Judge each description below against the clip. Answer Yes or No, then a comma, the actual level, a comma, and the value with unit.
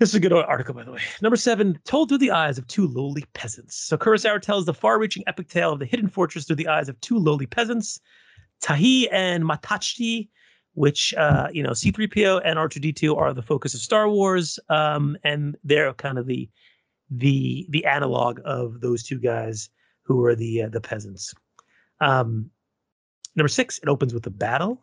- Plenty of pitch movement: Yes, wide, 7.8 semitones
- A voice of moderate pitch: Yes, medium, 150 Hz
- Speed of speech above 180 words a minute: Yes, average, 190 wpm